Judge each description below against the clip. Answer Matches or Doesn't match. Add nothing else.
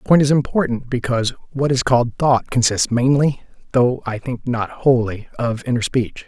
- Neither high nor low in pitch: Doesn't match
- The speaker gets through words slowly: Doesn't match